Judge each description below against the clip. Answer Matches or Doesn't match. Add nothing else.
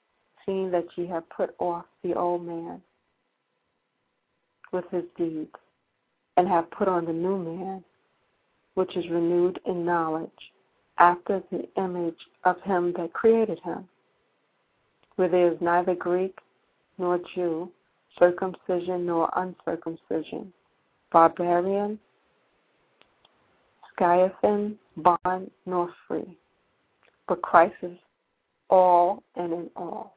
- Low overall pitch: Doesn't match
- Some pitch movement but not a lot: Doesn't match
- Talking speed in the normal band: Doesn't match